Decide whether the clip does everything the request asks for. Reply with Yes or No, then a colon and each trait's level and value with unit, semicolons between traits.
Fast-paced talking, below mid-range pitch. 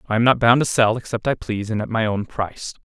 Yes: fast, 295 wpm; low, 115 Hz